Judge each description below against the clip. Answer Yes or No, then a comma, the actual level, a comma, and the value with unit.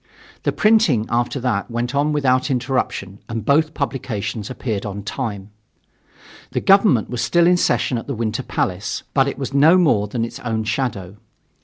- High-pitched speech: No, low, 125 Hz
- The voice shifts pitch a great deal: No, average, 4.7 semitones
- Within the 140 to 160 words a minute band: No, average, 170 wpm